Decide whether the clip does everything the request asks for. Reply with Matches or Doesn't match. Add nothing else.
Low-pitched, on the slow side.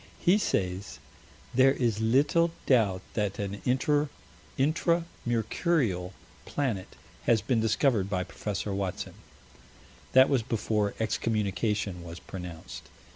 Matches